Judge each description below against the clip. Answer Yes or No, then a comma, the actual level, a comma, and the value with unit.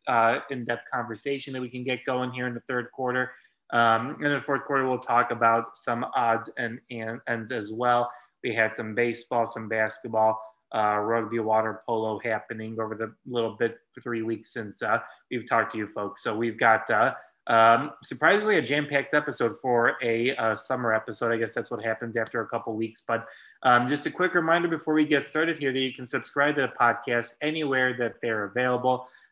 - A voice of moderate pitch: No, low, 120 Hz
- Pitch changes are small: Yes, narrow, 2.2 semitones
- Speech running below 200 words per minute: No, fast, 205 wpm